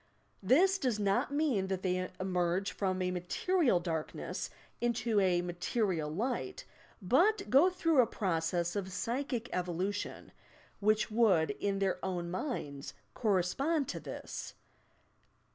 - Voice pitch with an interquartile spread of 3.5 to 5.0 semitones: No, wide, 5.5 semitones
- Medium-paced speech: No, slow, 125 wpm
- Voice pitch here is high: Yes, high, 200 Hz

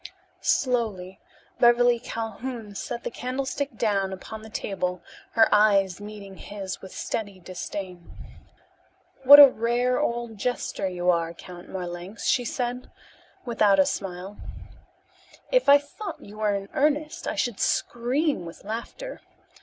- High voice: Yes, high, 215 Hz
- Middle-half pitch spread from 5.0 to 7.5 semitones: No, average, 4.3 semitones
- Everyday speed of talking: No, slow, 130 wpm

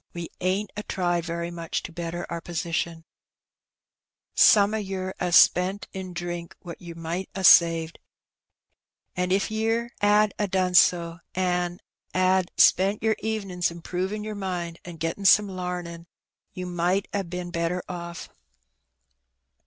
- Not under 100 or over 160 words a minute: Yes, average, 145 wpm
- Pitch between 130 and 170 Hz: No, medium, 180 Hz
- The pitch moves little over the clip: Yes, narrow, 2.1 semitones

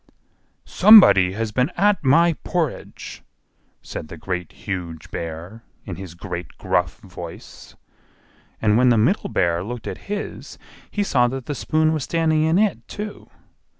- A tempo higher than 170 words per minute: No, average, 150 wpm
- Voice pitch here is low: Yes, low, 125 Hz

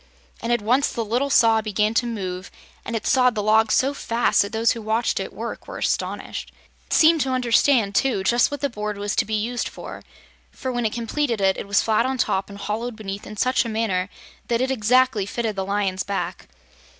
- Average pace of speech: No, fast, 220 wpm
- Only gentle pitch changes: No, average, 3.1 semitones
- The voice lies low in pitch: No, high, 225 Hz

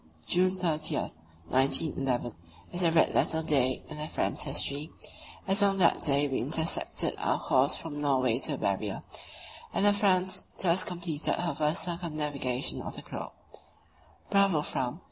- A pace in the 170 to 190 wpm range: No, average, 150 wpm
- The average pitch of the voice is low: No, medium, 155 Hz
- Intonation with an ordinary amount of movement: Yes, average, 4.2 semitones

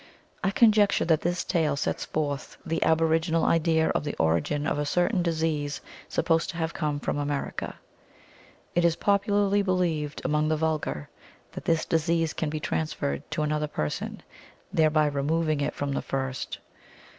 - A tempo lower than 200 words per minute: Yes, average, 155 wpm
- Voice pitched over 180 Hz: No, medium, 155 Hz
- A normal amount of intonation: No, narrow, 2.3 semitones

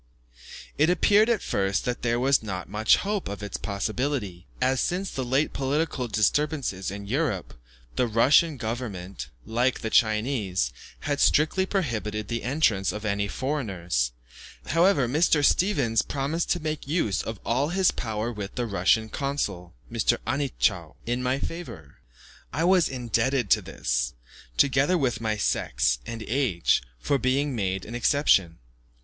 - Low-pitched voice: Yes, low, 120 Hz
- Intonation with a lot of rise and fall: Yes, wide, 6.0 semitones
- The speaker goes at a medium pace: Yes, average, 145 wpm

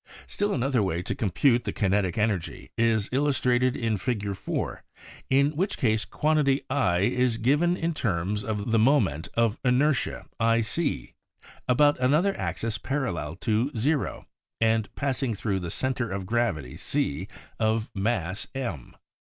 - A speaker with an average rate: Yes, average, 150 wpm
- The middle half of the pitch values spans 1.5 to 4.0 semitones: No, average, 4.9 semitones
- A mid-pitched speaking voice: No, low, 115 Hz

